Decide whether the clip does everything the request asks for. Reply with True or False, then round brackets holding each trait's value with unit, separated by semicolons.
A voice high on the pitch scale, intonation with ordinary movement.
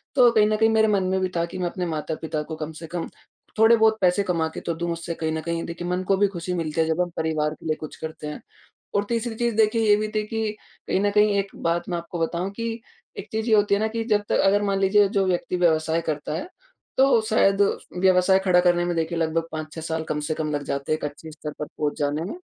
False (175 Hz; 4.4 semitones)